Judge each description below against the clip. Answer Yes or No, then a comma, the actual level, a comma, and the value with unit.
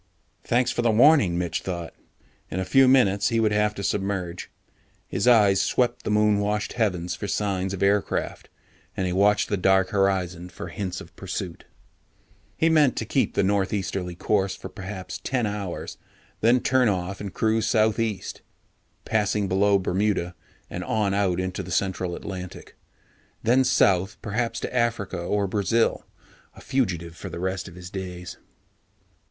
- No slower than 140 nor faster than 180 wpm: Yes, average, 160 wpm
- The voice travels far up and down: No, average, 2.8 semitones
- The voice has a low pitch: Yes, low, 100 Hz